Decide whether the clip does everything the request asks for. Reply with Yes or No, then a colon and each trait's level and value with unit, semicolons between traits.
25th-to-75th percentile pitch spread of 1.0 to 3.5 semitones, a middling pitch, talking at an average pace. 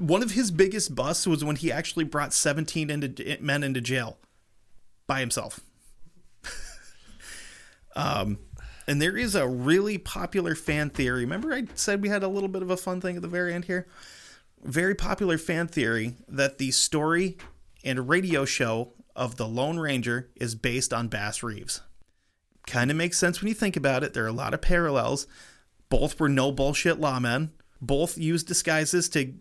No: average, 5.1 semitones; medium, 155 Hz; average, 175 wpm